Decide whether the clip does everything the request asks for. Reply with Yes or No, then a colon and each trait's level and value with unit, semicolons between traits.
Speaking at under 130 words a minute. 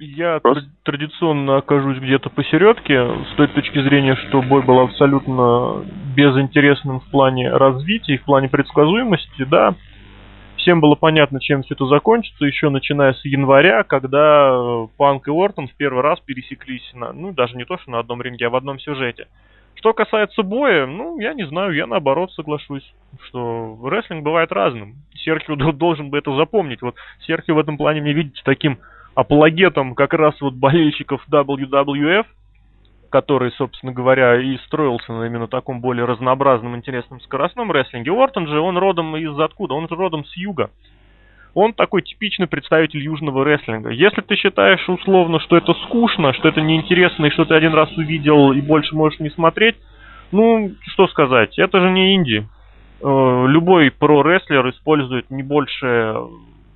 No: fast, 160 wpm